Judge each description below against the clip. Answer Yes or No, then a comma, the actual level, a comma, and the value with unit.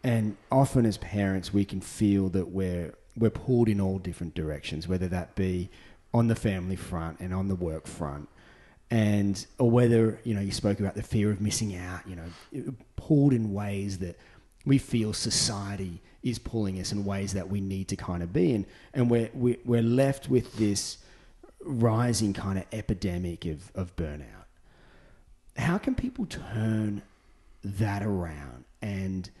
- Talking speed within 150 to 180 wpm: Yes, average, 165 wpm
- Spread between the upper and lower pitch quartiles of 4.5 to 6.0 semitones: No, average, 3.6 semitones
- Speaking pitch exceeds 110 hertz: No, low, 100 Hz